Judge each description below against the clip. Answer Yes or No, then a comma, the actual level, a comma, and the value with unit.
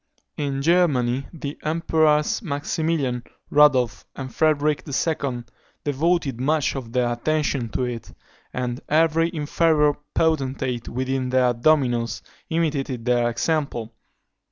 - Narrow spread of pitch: No, average, 3.9 semitones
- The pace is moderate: No, slow, 105 wpm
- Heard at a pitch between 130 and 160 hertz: Yes, medium, 140 Hz